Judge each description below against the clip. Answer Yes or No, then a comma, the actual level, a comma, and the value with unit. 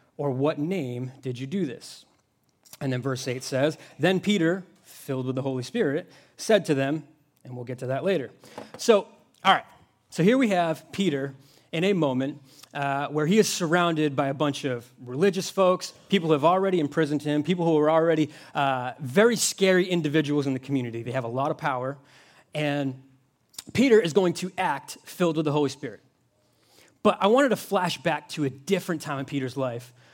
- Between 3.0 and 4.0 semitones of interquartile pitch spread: No, average, 4.7 semitones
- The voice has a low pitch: No, medium, 150 Hz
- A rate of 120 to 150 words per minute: No, average, 195 wpm